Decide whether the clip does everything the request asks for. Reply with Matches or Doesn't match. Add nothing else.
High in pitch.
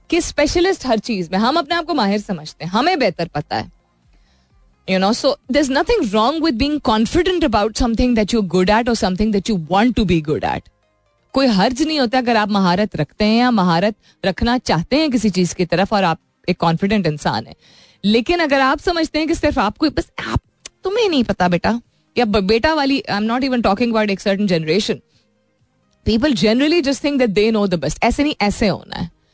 Matches